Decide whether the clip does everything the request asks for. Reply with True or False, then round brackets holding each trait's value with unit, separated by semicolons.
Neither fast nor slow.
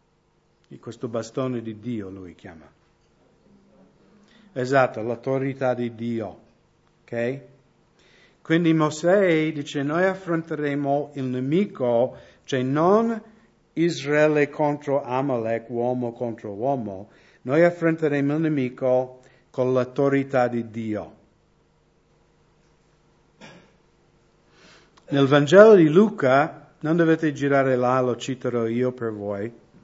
False (95 wpm)